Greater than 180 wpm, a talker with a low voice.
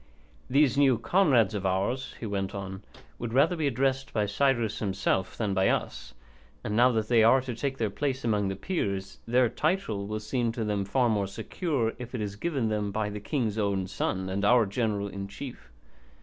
Yes: average, 200 wpm; low, 110 Hz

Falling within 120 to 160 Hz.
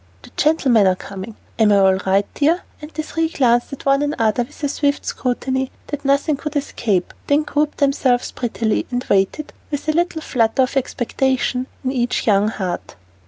No: very high, 260 Hz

